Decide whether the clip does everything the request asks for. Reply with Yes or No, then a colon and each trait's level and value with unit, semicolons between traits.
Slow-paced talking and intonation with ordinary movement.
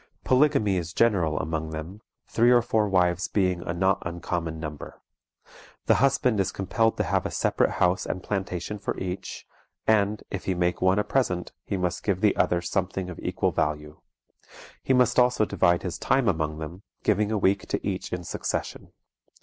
No: average, 180 wpm; average, 3.4 semitones